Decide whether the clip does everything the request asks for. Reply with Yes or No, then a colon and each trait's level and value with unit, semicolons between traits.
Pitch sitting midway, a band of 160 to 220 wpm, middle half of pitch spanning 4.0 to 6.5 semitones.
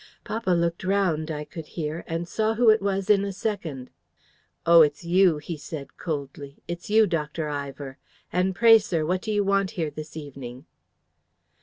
Yes: medium, 170 Hz; average, 175 wpm; average, 4.6 semitones